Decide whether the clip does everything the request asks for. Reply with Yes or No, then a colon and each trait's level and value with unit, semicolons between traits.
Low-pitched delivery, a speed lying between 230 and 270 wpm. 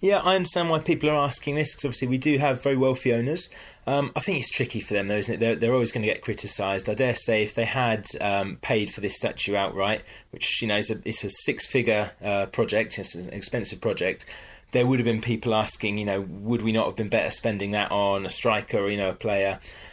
Yes: low, 110 Hz; fast, 245 wpm